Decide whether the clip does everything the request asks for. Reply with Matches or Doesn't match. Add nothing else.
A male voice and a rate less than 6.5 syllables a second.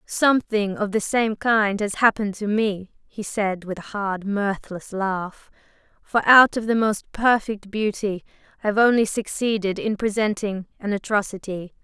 Doesn't match